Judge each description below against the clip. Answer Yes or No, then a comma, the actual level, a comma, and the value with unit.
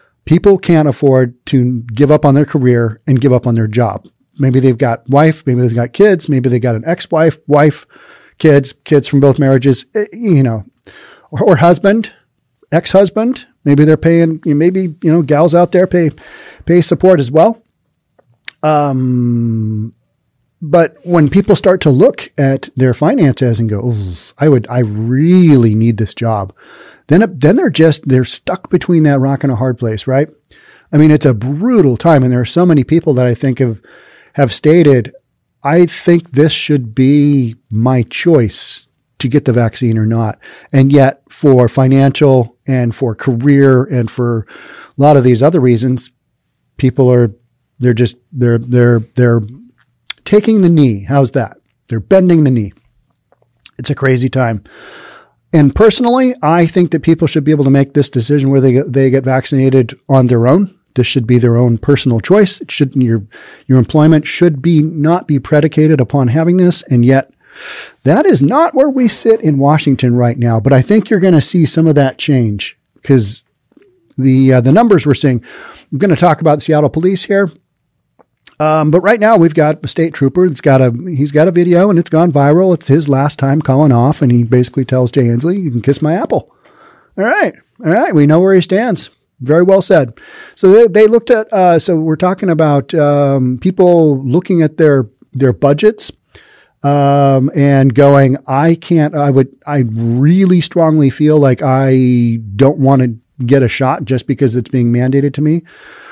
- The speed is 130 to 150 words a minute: No, average, 185 wpm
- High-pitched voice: No, medium, 140 Hz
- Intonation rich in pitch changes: No, average, 4.6 semitones